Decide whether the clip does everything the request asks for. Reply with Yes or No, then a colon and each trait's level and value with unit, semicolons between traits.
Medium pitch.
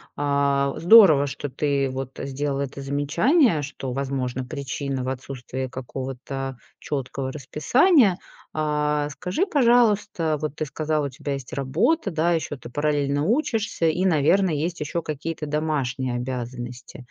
Yes: medium, 145 Hz